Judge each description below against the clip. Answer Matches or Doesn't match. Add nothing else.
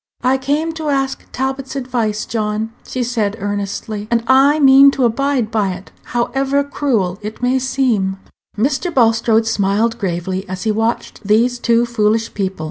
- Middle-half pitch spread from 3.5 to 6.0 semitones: Matches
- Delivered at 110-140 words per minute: Doesn't match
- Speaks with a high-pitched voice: Matches